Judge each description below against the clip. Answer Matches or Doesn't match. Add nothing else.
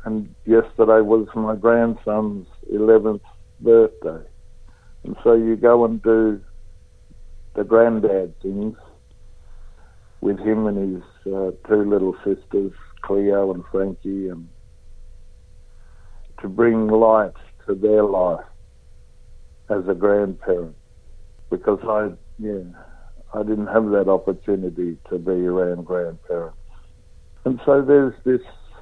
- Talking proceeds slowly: Matches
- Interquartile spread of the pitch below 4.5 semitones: Matches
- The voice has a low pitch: Matches